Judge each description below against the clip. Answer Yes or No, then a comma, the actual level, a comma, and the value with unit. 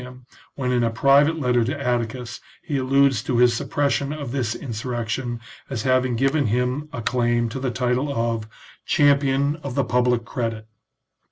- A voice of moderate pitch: No, low, 125 Hz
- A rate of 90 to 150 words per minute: No, average, 165 wpm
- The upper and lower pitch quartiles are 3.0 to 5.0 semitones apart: No, narrow, 2.6 semitones